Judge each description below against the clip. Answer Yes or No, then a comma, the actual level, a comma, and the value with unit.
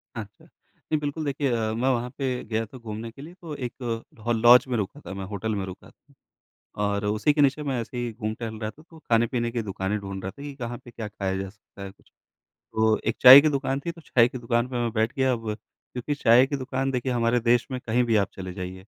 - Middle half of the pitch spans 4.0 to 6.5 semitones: No, average, 3.4 semitones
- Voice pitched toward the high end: No, low, 120 Hz